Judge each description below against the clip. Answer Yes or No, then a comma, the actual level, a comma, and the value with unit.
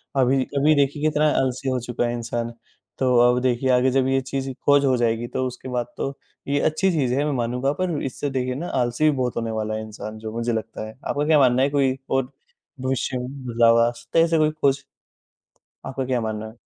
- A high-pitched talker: No, low, 130 Hz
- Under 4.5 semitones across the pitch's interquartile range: Yes, average, 2.7 semitones